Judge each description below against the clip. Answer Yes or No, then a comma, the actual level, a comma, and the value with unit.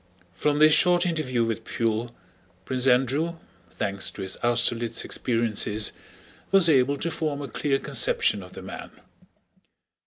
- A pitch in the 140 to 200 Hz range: No, low, 130 Hz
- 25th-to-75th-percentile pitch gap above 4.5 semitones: Yes, average, 5.2 semitones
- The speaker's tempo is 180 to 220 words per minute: No, slow, 135 wpm